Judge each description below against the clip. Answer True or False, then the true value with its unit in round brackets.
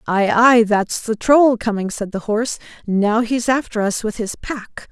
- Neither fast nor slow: True (195 wpm)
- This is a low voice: False (220 Hz)